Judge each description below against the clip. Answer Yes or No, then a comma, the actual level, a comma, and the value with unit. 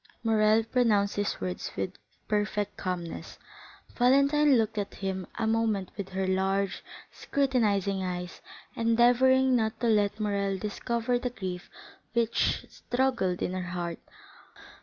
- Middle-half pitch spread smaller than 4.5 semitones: Yes, average, 3.7 semitones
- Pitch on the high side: Yes, high, 210 Hz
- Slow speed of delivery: Yes, slow, 125 wpm